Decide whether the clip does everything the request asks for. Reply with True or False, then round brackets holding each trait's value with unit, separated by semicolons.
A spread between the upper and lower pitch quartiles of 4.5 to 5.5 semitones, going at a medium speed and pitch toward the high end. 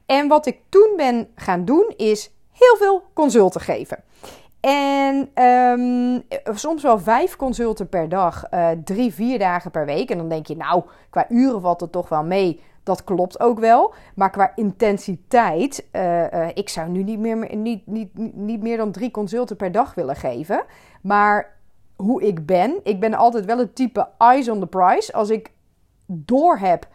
True (4.8 semitones; 180 wpm; 220 Hz)